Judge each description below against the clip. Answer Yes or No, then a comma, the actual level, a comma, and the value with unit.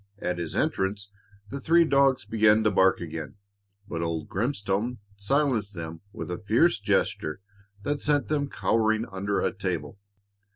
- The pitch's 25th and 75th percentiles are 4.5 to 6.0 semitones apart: Yes, wide, 5.6 semitones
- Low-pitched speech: Yes, low, 105 Hz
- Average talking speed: Yes, average, 150 wpm